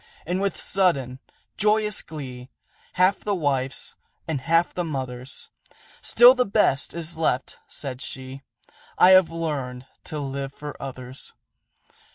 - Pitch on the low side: No, medium, 150 Hz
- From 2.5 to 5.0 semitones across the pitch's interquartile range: No, wide, 5.5 semitones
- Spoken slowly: Yes, slow, 130 wpm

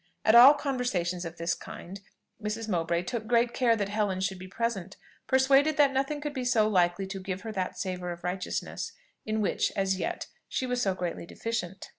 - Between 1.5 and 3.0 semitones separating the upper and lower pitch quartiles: No, average, 5.0 semitones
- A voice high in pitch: Yes, high, 205 Hz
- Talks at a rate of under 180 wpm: No, average, 195 wpm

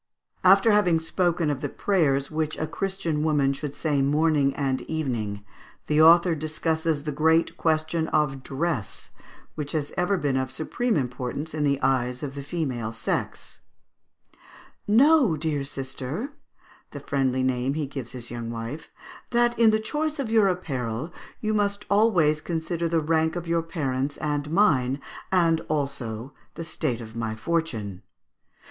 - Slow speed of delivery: No, average, 155 wpm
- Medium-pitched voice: Yes, medium, 155 Hz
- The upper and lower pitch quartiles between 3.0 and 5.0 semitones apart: Yes, average, 4.0 semitones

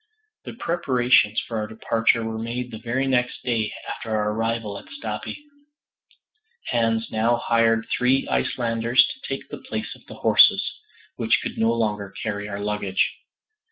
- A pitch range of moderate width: No, narrow, 2.0 semitones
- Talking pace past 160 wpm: No, average, 155 wpm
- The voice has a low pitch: Yes, low, 115 Hz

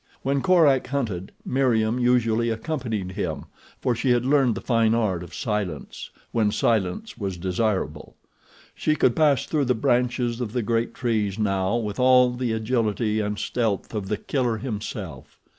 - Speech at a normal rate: Yes, average, 160 wpm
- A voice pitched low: Yes, low, 115 Hz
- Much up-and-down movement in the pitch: No, average, 3.2 semitones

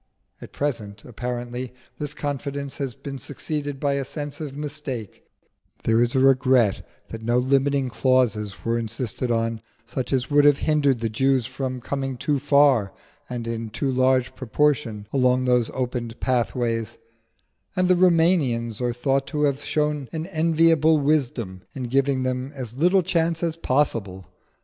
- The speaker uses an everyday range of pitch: Yes, average, 3.3 semitones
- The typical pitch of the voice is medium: No, low, 130 Hz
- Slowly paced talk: No, average, 155 wpm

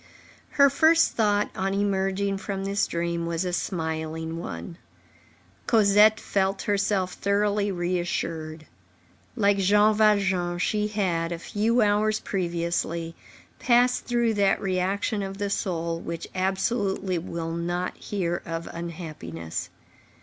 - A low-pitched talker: No, high, 190 Hz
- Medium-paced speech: No, slow, 120 wpm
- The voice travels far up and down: No, average, 3.4 semitones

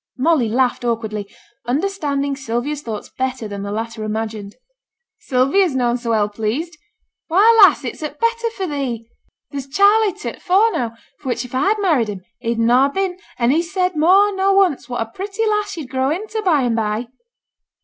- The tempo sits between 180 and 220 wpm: Yes, average, 185 wpm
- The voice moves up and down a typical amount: No, wide, 8.5 semitones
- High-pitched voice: Yes, very high, 275 Hz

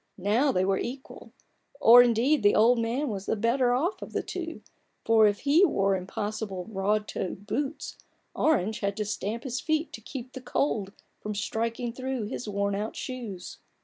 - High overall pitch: Yes, high, 225 Hz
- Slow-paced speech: No, average, 180 wpm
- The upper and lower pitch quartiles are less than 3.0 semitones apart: No, average, 4.0 semitones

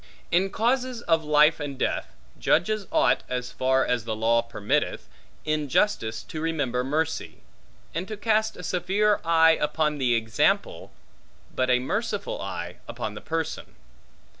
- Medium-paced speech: Yes, average, 145 wpm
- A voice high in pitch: No, medium, 155 Hz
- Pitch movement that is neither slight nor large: No, wide, 7.2 semitones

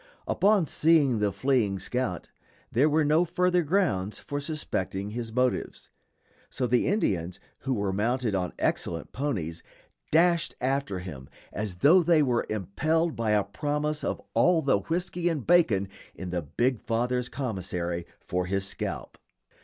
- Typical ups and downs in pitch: No, wide, 7.9 semitones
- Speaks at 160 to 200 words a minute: No, average, 145 wpm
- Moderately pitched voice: No, low, 125 Hz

